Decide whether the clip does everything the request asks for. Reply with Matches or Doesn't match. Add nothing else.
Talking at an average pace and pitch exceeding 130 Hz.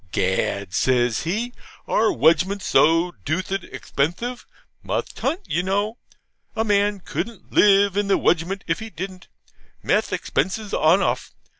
Doesn't match